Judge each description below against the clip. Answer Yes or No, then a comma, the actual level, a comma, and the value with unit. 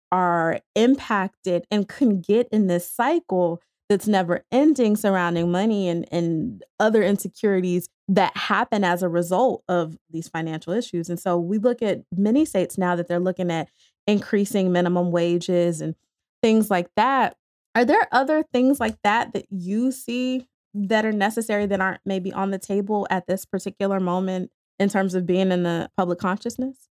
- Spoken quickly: No, average, 165 wpm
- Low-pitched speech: No, high, 195 Hz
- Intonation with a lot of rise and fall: No, average, 3.5 semitones